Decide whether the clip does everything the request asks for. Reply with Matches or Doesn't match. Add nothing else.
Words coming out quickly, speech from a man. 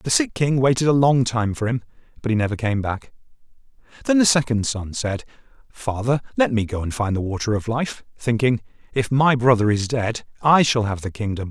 Matches